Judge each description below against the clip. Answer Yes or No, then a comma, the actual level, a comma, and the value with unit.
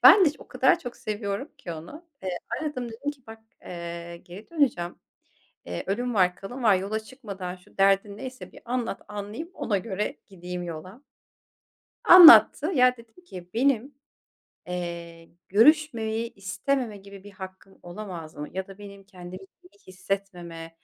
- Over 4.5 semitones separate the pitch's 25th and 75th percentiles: Yes, average, 5.1 semitones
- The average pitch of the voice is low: No, high, 200 Hz